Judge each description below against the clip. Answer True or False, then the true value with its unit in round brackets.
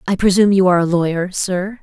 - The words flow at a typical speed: False (230 wpm)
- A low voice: False (185 Hz)